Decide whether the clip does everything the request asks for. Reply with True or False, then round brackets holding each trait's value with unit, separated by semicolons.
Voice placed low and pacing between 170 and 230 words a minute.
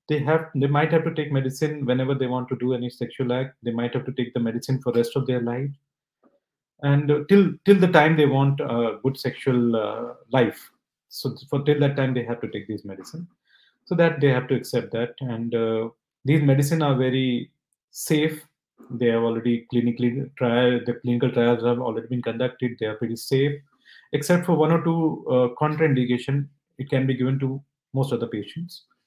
True (130 Hz; 205 wpm)